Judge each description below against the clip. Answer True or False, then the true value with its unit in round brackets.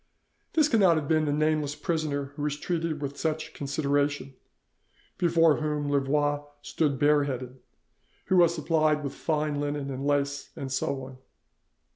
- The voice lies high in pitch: False (145 Hz)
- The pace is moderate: True (150 wpm)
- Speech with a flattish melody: True (1.7 semitones)